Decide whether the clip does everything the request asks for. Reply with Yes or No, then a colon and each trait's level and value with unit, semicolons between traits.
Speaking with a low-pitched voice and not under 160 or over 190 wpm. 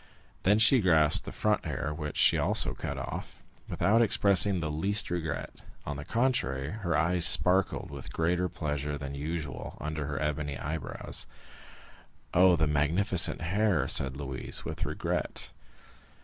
No: very low, 80 Hz; average, 150 wpm